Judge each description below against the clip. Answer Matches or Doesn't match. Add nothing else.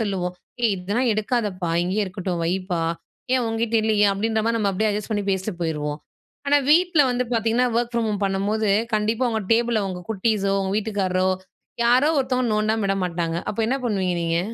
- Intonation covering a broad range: Doesn't match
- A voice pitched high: Matches